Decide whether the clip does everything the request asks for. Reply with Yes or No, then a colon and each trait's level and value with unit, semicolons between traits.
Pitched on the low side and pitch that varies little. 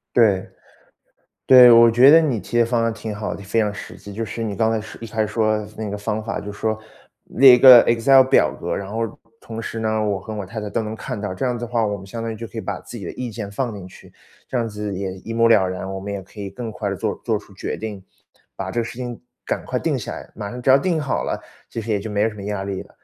Yes: low, 110 Hz; narrow, 2.3 semitones